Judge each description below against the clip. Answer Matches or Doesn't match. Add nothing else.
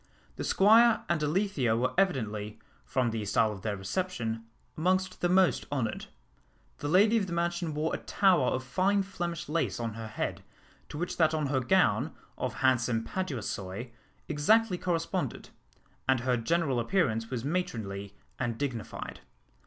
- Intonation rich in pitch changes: Matches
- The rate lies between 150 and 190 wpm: Matches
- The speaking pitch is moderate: Matches